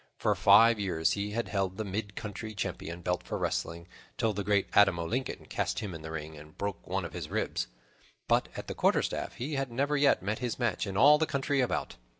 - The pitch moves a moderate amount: Yes, average, 4.7 semitones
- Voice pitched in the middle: No, low, 100 Hz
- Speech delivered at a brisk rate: Yes, fast, 220 wpm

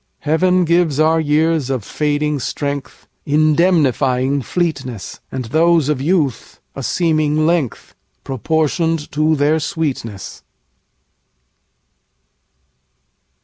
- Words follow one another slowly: Yes, slow, 75 wpm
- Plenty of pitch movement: No, average, 2.9 semitones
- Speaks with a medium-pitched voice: Yes, medium, 150 Hz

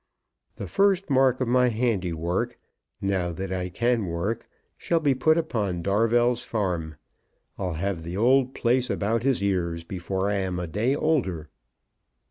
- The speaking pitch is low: Yes, low, 100 Hz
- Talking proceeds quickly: No, average, 150 wpm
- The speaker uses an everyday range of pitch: No, wide, 5.7 semitones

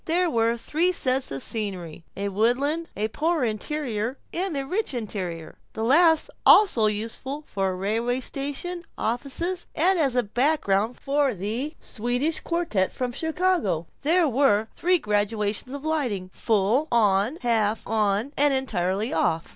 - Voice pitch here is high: Yes, high, 245 Hz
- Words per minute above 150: No, average, 140 wpm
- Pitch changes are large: Yes, wide, 6.5 semitones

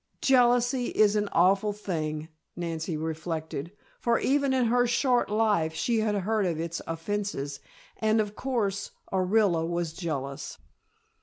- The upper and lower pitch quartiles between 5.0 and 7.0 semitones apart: Yes, wide, 5.5 semitones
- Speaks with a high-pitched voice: Yes, high, 200 Hz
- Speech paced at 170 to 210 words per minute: No, slow, 135 wpm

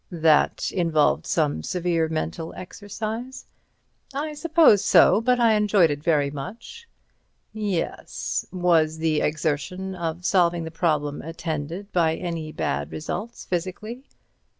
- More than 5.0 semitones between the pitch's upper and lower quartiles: No, average, 4.7 semitones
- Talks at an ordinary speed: No, slow, 120 wpm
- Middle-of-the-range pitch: Yes, medium, 175 Hz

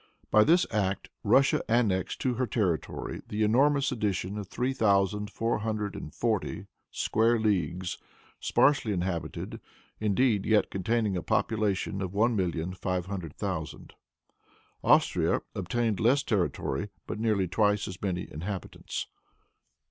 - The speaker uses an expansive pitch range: No, average, 3.4 semitones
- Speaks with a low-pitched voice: Yes, low, 105 Hz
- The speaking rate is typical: No, slow, 130 wpm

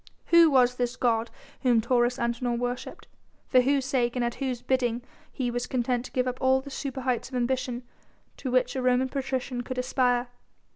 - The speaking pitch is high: Yes, very high, 250 Hz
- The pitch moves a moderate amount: No, narrow, 1.3 semitones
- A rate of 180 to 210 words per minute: Yes, average, 185 wpm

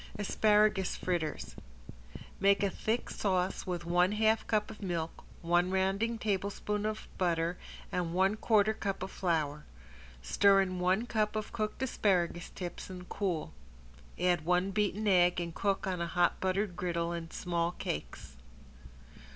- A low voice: No, medium, 185 Hz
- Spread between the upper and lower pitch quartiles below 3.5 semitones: Yes, average, 3.1 semitones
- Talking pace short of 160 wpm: Yes, average, 145 wpm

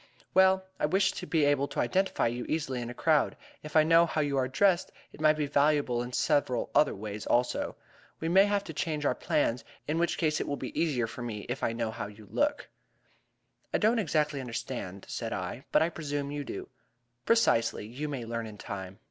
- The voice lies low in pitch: No, medium, 145 Hz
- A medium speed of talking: No, fast, 215 wpm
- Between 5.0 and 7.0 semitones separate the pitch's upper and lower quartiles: Yes, average, 5.3 semitones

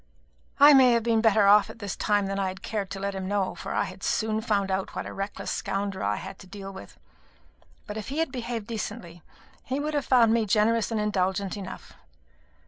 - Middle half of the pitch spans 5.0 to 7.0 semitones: No, average, 2.8 semitones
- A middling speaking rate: No, fast, 225 wpm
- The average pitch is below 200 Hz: No, high, 210 Hz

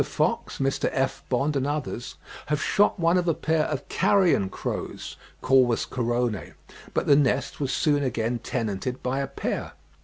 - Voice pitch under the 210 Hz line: Yes, low, 135 Hz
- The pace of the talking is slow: No, average, 160 wpm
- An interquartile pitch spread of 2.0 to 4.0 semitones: Yes, average, 3.4 semitones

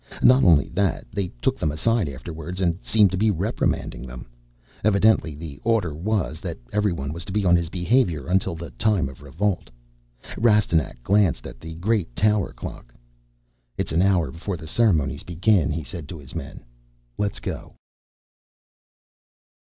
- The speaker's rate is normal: Yes, average, 160 wpm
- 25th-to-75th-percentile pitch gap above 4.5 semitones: Yes, average, 4.9 semitones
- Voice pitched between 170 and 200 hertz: No, very low, 85 Hz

